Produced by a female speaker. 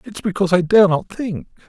No: male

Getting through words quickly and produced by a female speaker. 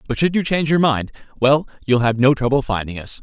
No: fast, 225 wpm; male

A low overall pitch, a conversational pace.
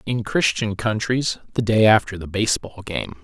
Yes: low, 105 Hz; average, 165 wpm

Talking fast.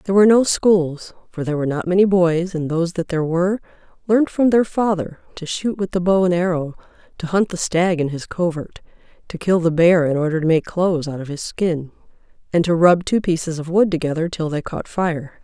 Yes: fast, 225 wpm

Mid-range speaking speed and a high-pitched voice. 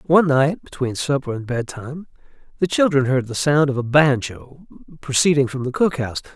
No: average, 180 wpm; medium, 140 Hz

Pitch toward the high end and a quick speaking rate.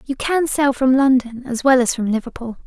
Yes: very high, 255 Hz; fast, 225 wpm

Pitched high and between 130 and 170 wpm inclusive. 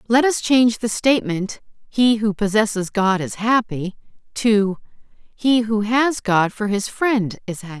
Yes: high, 220 Hz; average, 160 wpm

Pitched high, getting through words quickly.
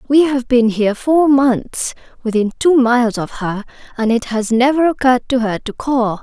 No: high, 245 Hz; average, 195 wpm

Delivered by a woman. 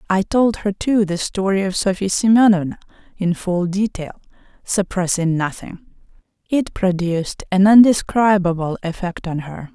Yes: female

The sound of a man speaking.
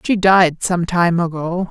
No: female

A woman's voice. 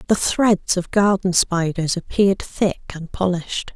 Yes: female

